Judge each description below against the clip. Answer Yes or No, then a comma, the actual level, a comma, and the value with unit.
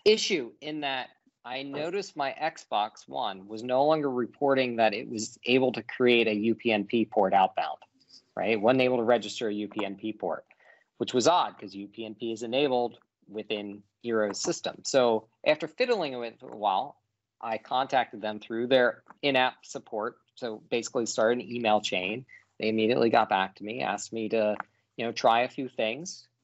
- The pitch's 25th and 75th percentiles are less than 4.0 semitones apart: Yes, average, 3.1 semitones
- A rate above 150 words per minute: Yes, average, 170 wpm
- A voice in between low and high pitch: No, low, 115 Hz